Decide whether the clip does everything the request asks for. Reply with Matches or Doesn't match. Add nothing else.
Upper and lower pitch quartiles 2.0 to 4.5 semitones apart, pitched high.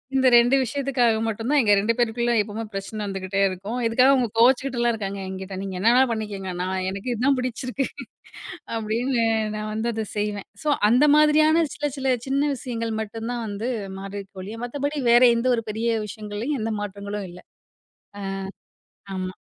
Matches